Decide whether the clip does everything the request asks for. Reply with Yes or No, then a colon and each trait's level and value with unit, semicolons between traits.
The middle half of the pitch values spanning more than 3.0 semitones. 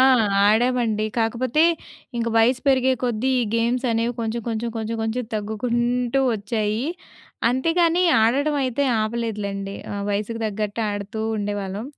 No: average, 2.7 semitones